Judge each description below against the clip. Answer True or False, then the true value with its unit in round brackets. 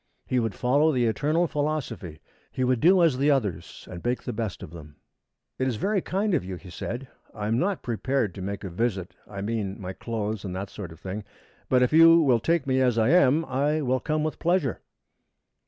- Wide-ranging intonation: True (6.8 semitones)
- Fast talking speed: True (220 wpm)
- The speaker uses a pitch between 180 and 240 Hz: False (125 Hz)